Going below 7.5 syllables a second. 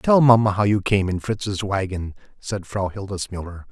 Yes: 4.7 syllables/s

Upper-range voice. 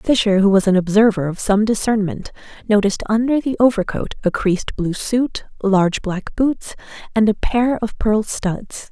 Yes: high, 210 Hz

